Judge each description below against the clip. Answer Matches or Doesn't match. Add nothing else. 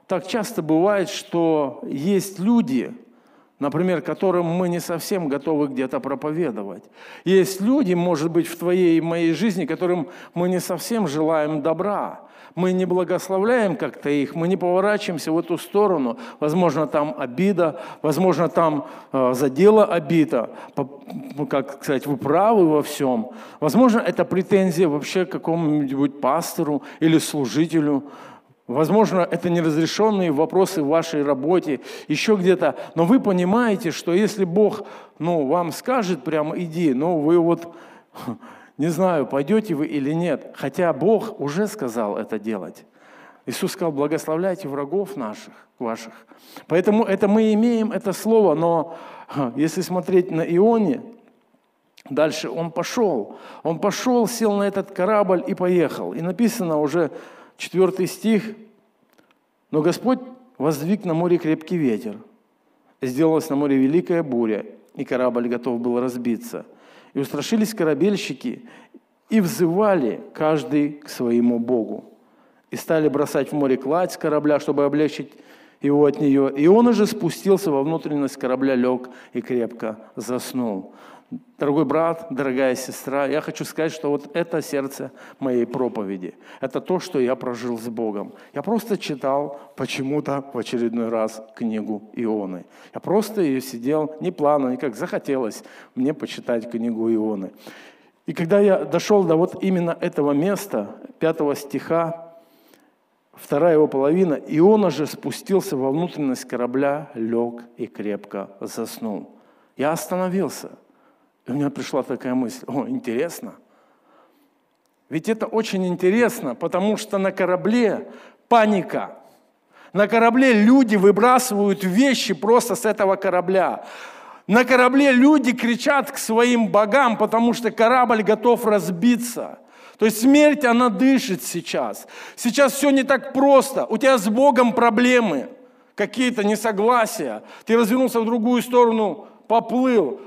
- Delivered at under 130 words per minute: Doesn't match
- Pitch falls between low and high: Matches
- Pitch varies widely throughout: Matches